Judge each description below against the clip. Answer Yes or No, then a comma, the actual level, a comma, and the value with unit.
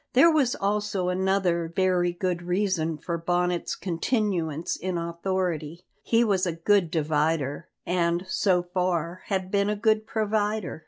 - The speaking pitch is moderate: Yes, medium, 180 Hz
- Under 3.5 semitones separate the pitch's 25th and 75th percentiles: Yes, average, 2.9 semitones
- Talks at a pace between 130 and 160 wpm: Yes, average, 140 wpm